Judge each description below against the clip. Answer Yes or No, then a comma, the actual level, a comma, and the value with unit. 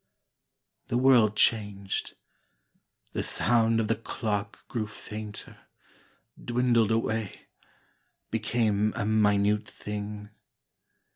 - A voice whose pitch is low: Yes, low, 110 Hz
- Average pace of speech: No, slow, 85 wpm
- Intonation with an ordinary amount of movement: No, narrow, 1.7 semitones